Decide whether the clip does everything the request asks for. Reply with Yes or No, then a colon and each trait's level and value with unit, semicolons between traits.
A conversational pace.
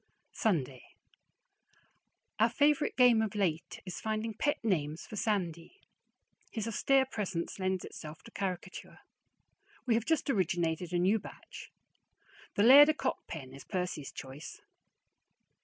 No: slow, 125 wpm